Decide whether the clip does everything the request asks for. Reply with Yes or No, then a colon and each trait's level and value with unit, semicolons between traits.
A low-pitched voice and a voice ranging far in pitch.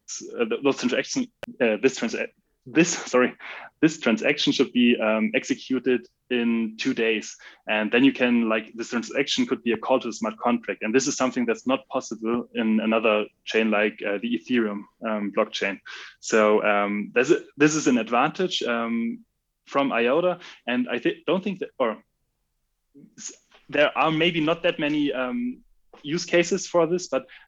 Yes: low, 125 Hz; wide, 5.7 semitones